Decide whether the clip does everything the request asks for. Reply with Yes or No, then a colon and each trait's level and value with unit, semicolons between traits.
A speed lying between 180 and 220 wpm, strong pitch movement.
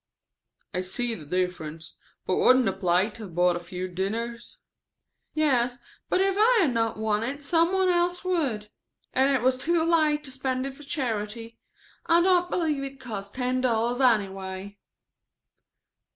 No: average, 165 wpm; wide, 6.6 semitones